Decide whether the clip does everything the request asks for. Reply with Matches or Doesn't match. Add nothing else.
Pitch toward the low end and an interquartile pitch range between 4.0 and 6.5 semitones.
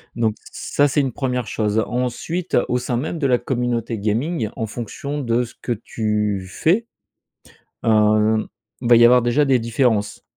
Doesn't match